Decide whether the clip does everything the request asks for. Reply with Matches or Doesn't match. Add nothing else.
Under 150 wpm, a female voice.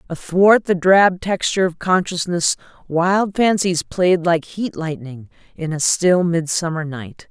Matches